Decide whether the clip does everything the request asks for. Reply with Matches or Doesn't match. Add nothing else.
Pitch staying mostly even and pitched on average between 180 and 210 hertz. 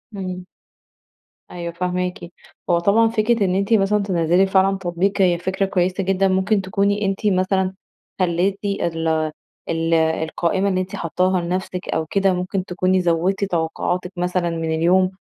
Matches